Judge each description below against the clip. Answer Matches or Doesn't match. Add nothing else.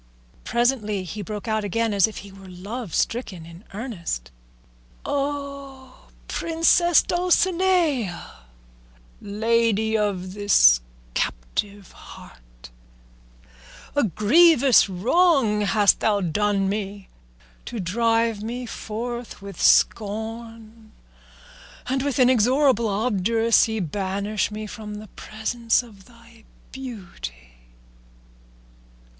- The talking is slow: Matches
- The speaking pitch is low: Doesn't match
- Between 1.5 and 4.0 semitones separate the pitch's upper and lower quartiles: Matches